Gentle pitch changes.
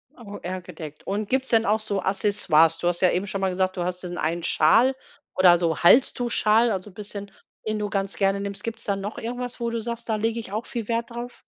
No: average, 3.9 semitones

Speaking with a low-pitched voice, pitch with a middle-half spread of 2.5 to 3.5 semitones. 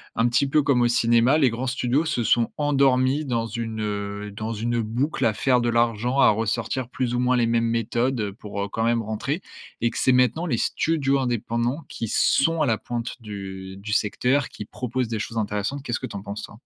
Yes: low, 120 Hz; average, 2.9 semitones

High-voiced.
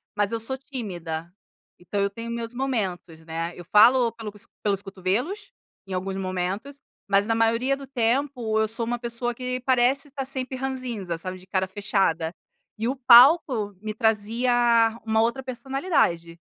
Yes: high, 225 Hz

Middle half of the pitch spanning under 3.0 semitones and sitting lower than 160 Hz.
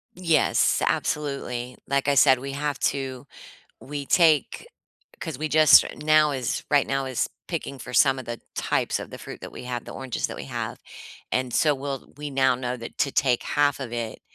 Yes: narrow, 2.6 semitones; low, 135 Hz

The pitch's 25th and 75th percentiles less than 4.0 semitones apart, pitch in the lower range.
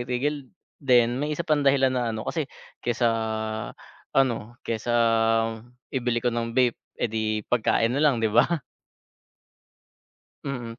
Yes: average, 2.9 semitones; low, 125 Hz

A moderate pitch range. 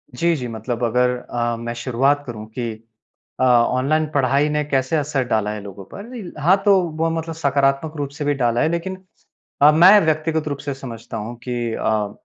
Yes: average, 4.7 semitones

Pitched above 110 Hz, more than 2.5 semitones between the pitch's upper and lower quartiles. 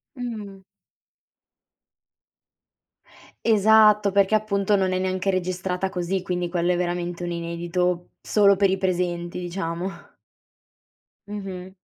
No: medium, 185 Hz; narrow, 2.0 semitones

